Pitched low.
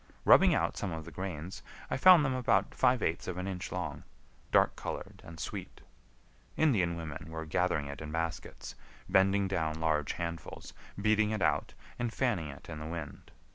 Yes: very low, 85 Hz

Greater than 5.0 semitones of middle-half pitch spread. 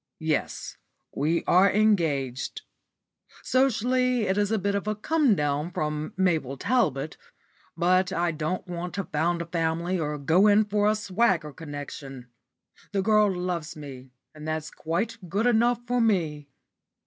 Yes: wide, 5.4 semitones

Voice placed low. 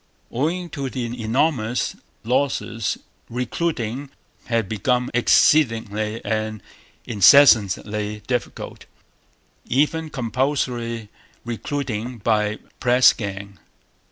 Yes: low, 120 Hz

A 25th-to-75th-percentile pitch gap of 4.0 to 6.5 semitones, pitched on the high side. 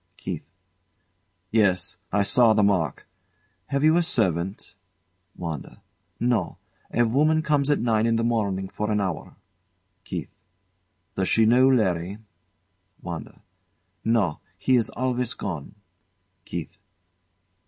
No: average, 5.0 semitones; low, 110 Hz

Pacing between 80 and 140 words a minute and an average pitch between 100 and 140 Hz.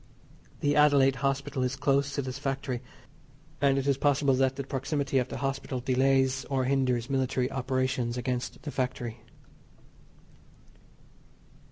Yes: slow, 135 wpm; low, 135 Hz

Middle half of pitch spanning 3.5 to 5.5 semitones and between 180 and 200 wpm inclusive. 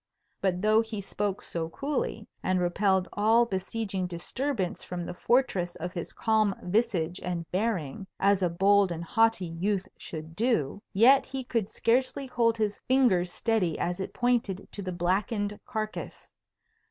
No: average, 4.1 semitones; average, 155 wpm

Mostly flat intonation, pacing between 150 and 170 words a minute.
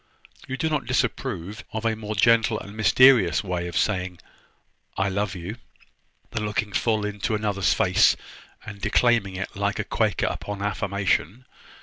Yes: narrow, 2.3 semitones; average, 155 wpm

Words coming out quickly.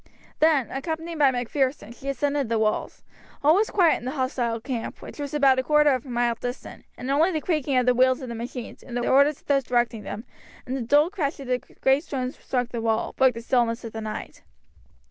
Yes: fast, 225 wpm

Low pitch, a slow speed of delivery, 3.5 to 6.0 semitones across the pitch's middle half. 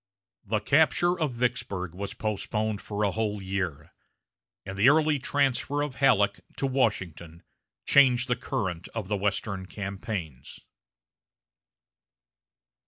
Yes: low, 105 Hz; slow, 110 wpm; average, 5.1 semitones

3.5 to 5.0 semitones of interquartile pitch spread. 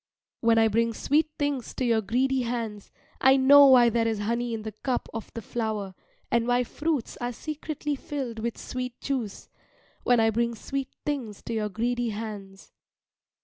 No: average, 2.9 semitones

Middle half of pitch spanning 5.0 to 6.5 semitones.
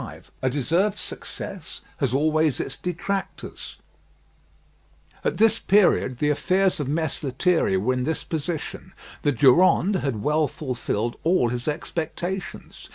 Yes: wide, 5.5 semitones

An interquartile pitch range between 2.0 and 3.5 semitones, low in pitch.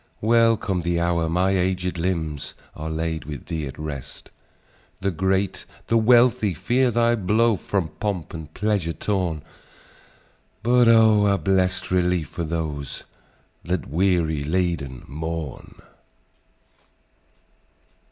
No: average, 4.1 semitones; very low, 90 Hz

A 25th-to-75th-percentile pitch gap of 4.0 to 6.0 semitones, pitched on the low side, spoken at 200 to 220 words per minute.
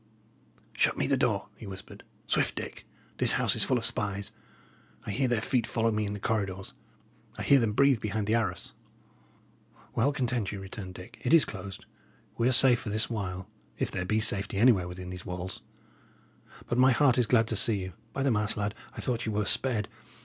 No: average, 3.5 semitones; low, 110 Hz; fast, 205 wpm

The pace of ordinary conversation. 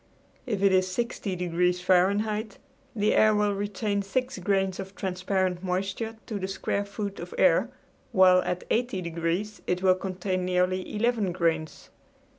Yes: average, 150 wpm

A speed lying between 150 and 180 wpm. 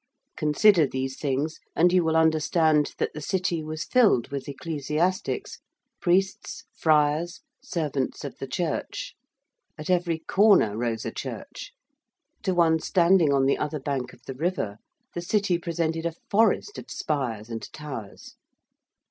No: average, 140 wpm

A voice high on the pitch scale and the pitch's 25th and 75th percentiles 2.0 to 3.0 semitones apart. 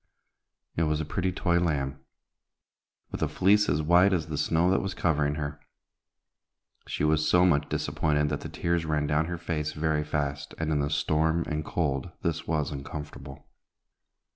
No: very low, 75 Hz; narrow, 2.4 semitones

